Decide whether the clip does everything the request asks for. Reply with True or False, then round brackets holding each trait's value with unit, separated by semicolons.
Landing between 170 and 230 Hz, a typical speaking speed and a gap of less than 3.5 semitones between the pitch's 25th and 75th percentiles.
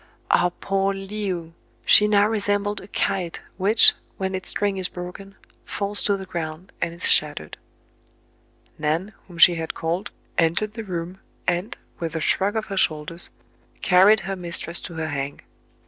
True (185 Hz; 160 wpm; 3.1 semitones)